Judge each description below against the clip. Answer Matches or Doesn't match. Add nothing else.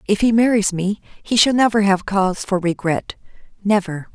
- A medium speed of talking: Matches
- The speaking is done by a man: Doesn't match